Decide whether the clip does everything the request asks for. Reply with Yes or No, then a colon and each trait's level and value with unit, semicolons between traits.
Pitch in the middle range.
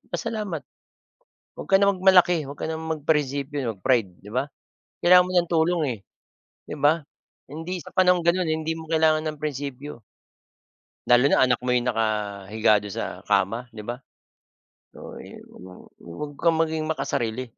Yes: medium, 150 Hz